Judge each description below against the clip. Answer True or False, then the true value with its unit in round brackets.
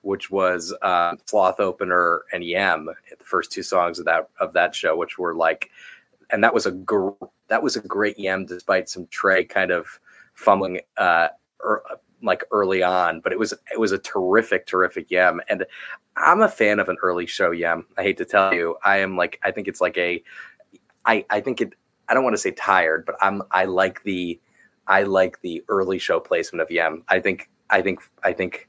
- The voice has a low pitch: True (95 Hz)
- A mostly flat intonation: True (1.9 semitones)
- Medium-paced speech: False (210 wpm)